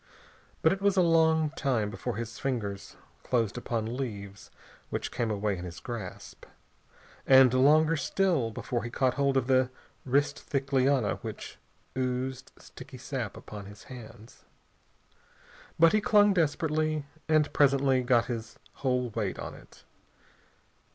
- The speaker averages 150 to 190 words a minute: No, average, 140 wpm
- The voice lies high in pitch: No, low, 130 Hz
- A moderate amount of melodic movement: Yes, average, 4.1 semitones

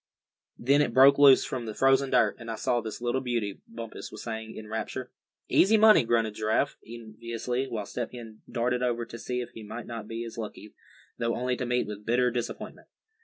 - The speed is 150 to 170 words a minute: No, fast, 205 wpm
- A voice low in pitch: Yes, low, 115 Hz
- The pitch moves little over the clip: Yes, narrow, 2.0 semitones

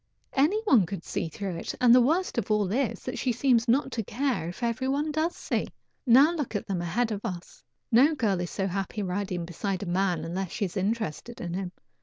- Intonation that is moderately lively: No, wide, 5.7 semitones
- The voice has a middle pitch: No, high, 215 Hz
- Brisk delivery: Yes, fast, 220 wpm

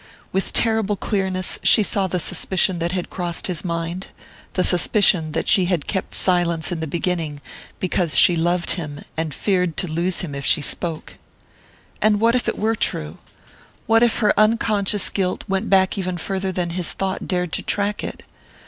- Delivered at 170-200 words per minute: Yes, average, 180 wpm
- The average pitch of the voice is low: No, medium, 185 Hz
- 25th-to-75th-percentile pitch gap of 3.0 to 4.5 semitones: No, narrow, 2.6 semitones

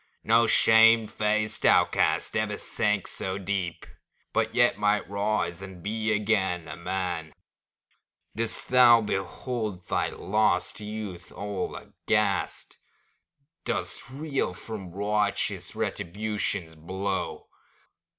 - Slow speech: Yes, slow, 100 wpm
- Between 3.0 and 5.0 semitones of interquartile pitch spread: No, narrow, 2.6 semitones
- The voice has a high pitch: No, low, 105 Hz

